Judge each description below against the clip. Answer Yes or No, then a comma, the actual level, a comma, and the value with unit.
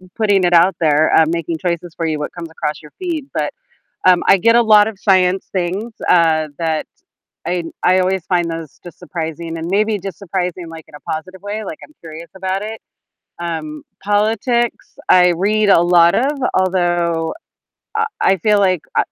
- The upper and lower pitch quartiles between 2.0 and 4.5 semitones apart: Yes, average, 3.4 semitones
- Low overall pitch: No, medium, 180 Hz